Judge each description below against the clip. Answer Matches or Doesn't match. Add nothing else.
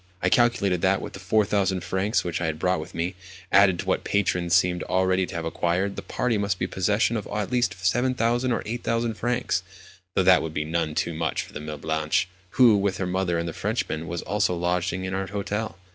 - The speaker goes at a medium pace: Doesn't match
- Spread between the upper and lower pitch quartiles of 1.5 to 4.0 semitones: Matches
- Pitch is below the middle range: Matches